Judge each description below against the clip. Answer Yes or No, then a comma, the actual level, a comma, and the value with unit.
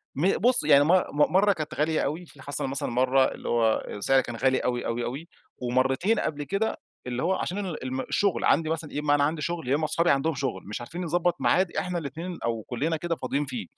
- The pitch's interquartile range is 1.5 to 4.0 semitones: No, average, 4.8 semitones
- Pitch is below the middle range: No, medium, 150 Hz